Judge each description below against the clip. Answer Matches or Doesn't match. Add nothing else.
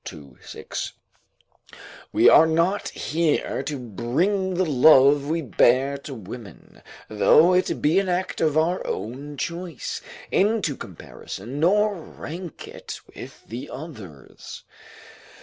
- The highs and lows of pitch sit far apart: Matches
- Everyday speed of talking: Doesn't match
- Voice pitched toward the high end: Doesn't match